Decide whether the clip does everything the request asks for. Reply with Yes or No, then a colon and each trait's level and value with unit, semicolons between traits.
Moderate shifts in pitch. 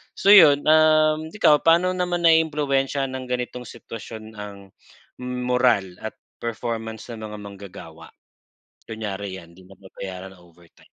No: wide, 6.9 semitones